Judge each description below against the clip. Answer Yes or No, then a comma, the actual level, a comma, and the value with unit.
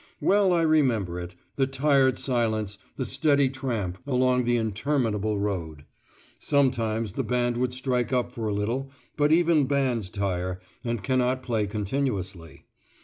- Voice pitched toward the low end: Yes, low, 120 Hz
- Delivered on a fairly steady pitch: No, average, 4.5 semitones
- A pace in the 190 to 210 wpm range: No, average, 145 wpm